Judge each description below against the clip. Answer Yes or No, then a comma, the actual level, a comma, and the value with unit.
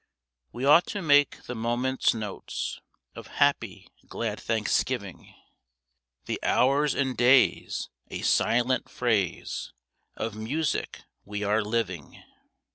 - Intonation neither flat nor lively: Yes, average, 3.6 semitones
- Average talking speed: No, slow, 110 wpm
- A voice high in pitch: No, low, 120 Hz